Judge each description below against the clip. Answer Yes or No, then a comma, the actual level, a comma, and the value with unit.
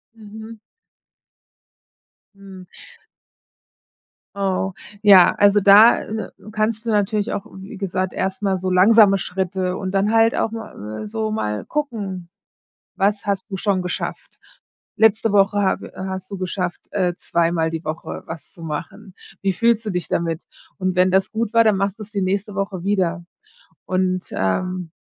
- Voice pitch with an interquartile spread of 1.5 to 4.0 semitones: Yes, narrow, 2.5 semitones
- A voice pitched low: No, high, 195 Hz